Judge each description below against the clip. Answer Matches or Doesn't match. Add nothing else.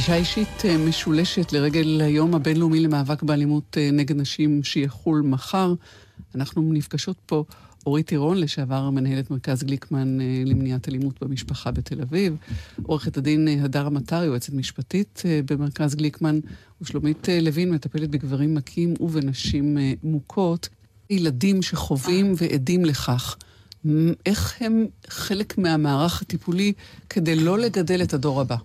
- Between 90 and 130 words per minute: Matches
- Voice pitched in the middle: Matches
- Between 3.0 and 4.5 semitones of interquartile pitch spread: Matches